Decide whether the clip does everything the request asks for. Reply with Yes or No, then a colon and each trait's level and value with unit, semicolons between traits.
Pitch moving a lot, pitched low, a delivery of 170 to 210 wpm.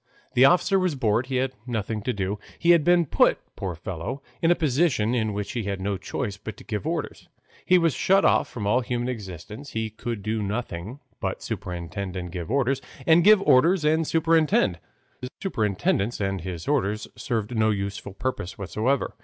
Yes: wide, 6.0 semitones; low, 115 Hz; average, 190 wpm